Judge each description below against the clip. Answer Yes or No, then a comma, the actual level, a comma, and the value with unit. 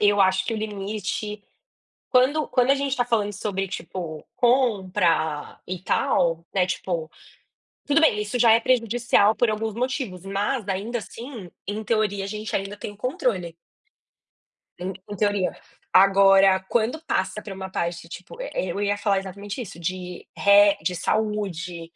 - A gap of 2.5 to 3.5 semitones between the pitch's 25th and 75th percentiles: Yes, average, 3.1 semitones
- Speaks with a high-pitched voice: Yes, high, 205 Hz